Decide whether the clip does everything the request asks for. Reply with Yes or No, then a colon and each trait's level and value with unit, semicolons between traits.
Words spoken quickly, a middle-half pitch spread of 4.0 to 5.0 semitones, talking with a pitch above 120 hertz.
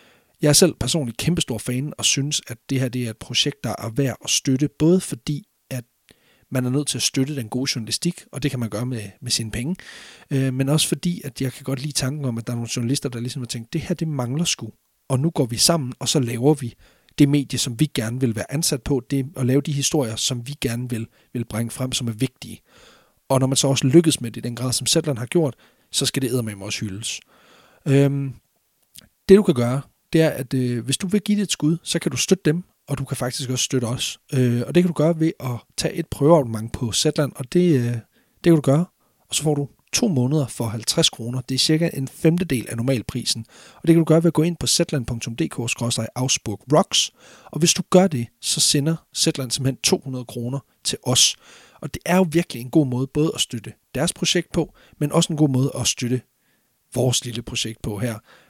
Yes: fast, 240 wpm; average, 4.3 semitones; low, 135 Hz